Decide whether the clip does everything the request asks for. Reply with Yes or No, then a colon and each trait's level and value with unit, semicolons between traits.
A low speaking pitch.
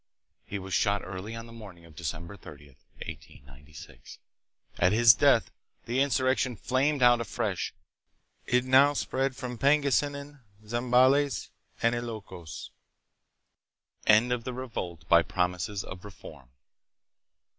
Yes: low, 115 Hz